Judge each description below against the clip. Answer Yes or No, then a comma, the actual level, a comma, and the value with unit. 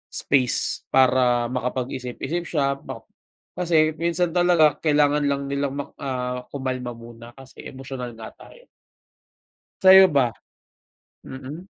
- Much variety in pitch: No, average, 3.7 semitones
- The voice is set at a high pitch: No, low, 135 Hz